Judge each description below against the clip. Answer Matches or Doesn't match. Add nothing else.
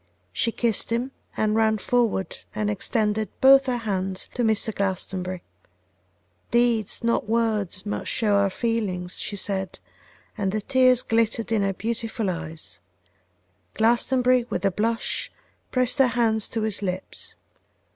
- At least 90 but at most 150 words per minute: Matches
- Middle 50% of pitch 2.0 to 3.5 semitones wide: Matches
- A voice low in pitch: Doesn't match